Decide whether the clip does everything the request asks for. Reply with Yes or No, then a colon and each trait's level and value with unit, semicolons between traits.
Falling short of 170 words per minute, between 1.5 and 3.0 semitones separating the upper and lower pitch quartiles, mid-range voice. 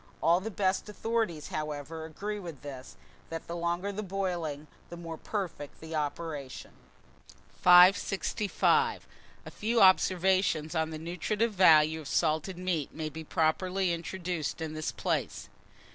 No: slow, 135 wpm; average, 3.4 semitones; medium, 170 Hz